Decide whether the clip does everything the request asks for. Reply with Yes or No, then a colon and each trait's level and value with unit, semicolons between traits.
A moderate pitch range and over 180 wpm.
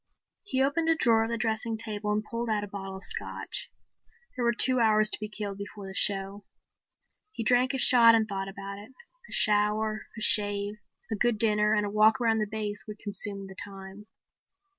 No: narrow, 2.1 semitones; fast, 205 wpm